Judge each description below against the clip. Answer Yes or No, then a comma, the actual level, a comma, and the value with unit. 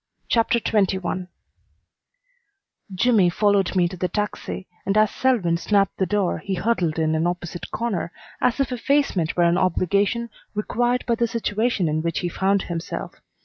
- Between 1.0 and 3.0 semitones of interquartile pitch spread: No, average, 4.7 semitones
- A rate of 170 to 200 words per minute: No, average, 155 wpm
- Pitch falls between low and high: No, high, 195 Hz